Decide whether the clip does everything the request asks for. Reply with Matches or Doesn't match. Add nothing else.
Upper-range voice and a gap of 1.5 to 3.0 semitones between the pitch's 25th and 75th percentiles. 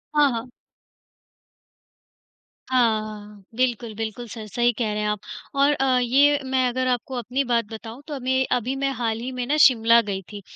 Matches